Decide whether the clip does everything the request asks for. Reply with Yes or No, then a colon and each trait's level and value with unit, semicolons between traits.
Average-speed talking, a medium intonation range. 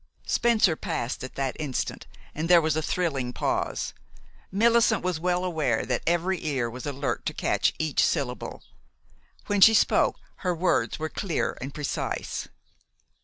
Yes: average, 150 wpm; average, 4.8 semitones